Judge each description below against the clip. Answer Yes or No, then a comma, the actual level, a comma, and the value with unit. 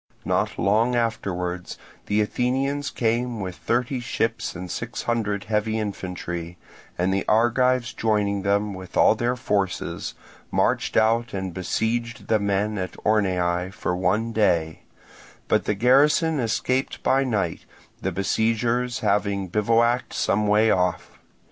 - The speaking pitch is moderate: No, low, 105 Hz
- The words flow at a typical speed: No, slow, 130 wpm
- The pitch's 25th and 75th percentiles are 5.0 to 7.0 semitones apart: No, average, 3.5 semitones